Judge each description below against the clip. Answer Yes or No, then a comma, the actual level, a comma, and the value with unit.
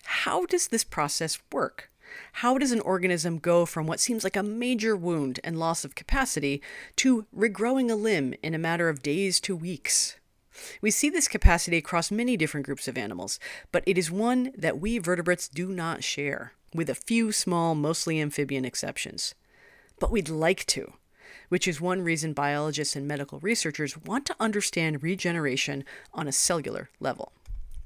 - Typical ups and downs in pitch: No, wide, 6.1 semitones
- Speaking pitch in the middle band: Yes, medium, 175 Hz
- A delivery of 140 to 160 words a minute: No, average, 170 wpm